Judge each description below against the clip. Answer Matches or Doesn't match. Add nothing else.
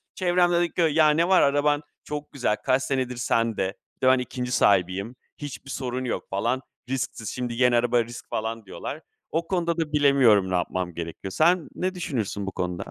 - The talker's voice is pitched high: Doesn't match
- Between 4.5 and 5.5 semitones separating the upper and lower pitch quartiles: Matches